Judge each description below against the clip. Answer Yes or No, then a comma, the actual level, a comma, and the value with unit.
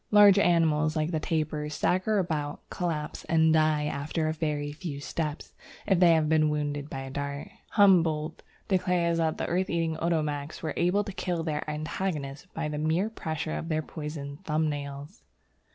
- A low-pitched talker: No, medium, 155 Hz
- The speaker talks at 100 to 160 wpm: No, average, 170 wpm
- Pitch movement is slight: Yes, narrow, 2.3 semitones